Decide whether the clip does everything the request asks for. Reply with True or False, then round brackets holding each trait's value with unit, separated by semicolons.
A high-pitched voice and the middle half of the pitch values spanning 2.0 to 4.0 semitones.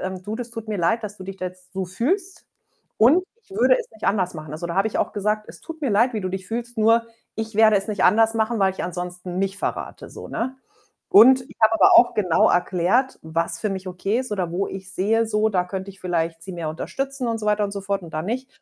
True (205 Hz; 3.7 semitones)